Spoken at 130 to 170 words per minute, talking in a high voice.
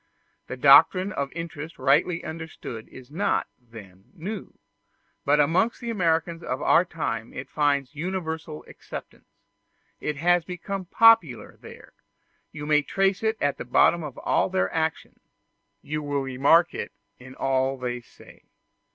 No: average, 145 wpm; medium, 155 Hz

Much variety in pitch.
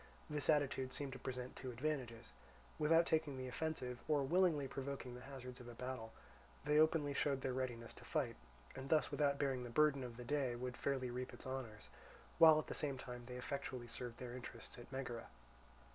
No: narrow, 2.6 semitones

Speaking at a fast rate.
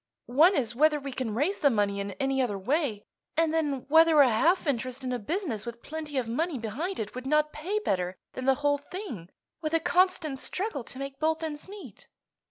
Yes: fast, 210 wpm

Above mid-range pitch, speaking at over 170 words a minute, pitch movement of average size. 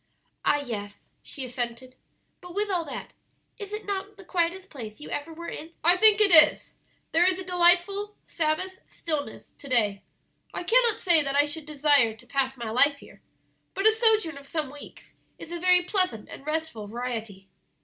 No: very high, 320 Hz; average, 185 wpm; wide, 6.1 semitones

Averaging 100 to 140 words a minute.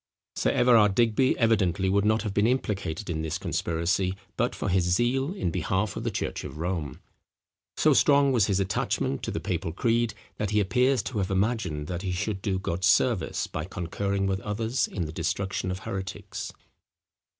No: average, 185 wpm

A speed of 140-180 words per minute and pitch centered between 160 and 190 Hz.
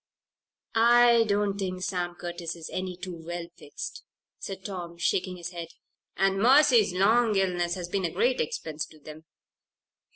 Yes: average, 155 wpm; medium, 185 Hz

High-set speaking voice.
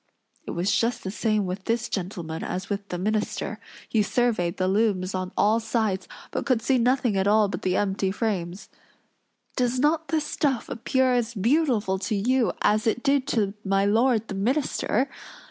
Yes: high, 215 Hz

